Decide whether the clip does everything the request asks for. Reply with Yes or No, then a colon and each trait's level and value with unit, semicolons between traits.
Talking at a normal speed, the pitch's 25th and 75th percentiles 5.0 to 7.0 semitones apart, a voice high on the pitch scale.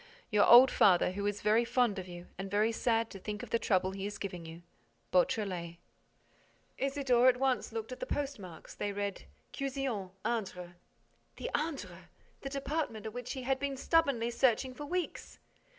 Yes: average, 170 wpm; average, 5.3 semitones; high, 225 Hz